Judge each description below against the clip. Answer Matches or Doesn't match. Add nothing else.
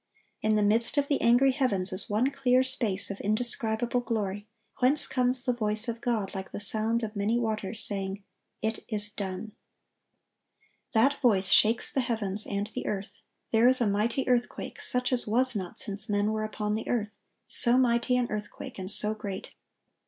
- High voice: Matches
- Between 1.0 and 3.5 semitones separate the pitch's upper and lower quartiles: Matches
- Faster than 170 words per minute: Matches